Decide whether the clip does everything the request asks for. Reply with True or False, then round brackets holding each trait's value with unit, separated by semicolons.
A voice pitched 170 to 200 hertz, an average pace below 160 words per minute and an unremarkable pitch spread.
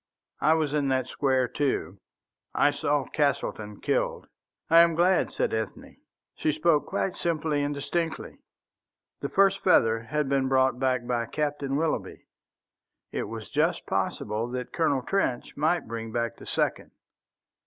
False (140 Hz; 145 wpm; 4.2 semitones)